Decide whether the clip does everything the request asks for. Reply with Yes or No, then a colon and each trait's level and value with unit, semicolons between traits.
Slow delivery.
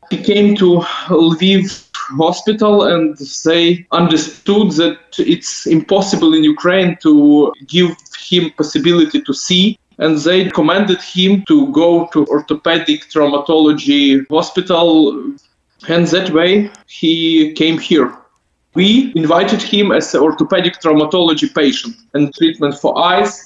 Yes: slow, 120 wpm